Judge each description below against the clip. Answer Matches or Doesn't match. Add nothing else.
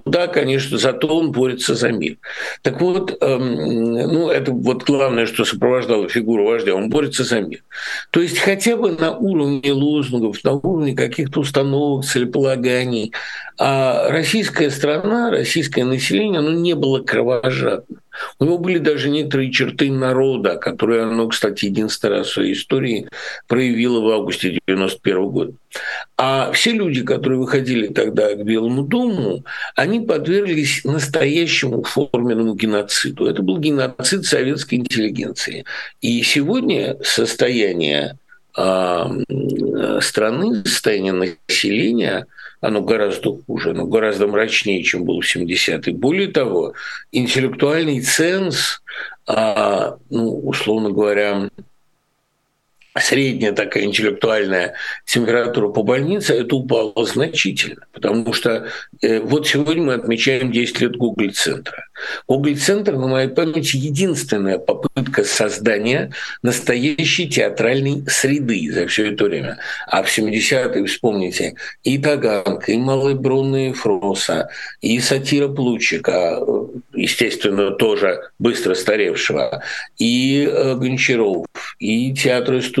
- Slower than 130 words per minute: Matches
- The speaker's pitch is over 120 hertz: Matches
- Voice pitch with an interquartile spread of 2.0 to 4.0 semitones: Doesn't match